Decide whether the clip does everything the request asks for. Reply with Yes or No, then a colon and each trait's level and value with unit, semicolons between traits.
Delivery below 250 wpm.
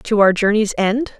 Yes: average, 200 wpm